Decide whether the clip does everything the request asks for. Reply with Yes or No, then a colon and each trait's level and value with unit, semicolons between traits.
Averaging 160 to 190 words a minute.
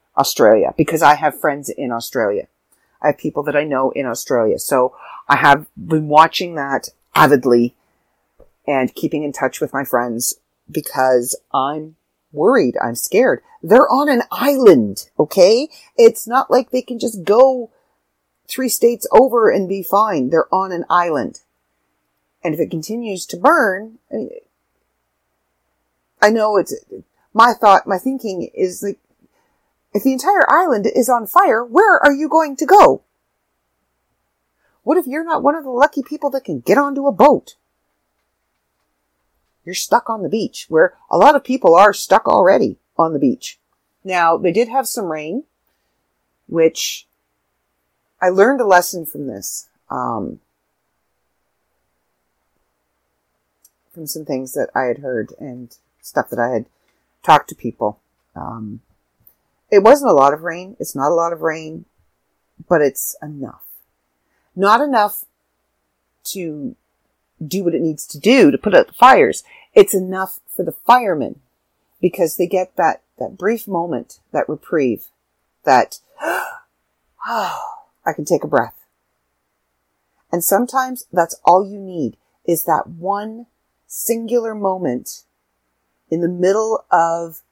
No: average, 145 wpm